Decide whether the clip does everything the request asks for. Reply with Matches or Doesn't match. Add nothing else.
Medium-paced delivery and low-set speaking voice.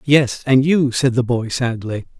Matches